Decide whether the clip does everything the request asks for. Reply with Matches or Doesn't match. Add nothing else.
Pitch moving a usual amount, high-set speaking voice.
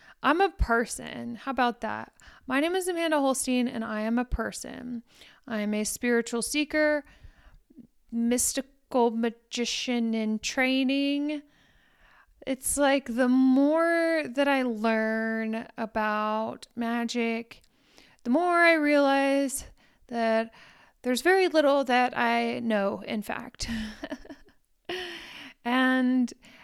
Matches